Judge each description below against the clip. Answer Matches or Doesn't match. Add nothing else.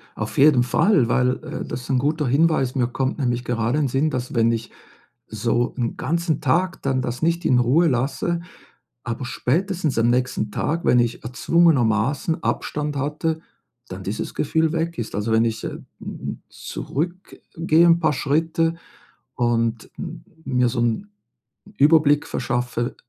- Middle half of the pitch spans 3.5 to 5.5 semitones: Matches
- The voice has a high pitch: Doesn't match